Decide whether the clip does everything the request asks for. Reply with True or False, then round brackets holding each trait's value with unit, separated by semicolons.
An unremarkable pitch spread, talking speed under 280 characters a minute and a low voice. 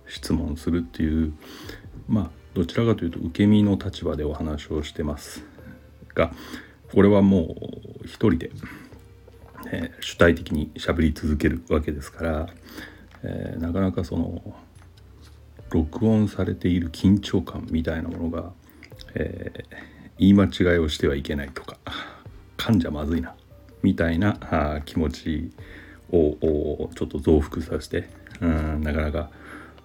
True (3.4 semitones; 270 characters per minute; 85 Hz)